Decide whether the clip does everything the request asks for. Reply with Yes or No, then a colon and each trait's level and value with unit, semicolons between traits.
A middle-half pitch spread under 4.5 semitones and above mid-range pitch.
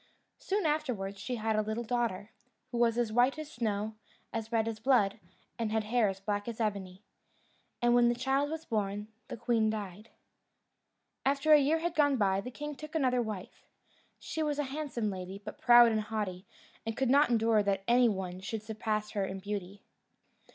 Yes: average, 3.6 semitones; high, 225 Hz